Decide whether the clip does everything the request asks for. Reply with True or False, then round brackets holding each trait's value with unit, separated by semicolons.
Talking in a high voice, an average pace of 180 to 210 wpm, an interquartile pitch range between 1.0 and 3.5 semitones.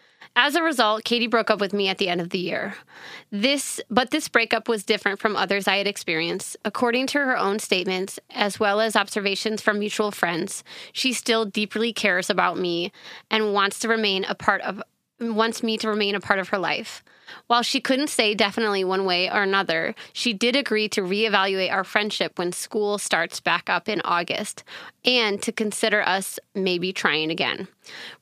True (210 Hz; 190 wpm; 2.8 semitones)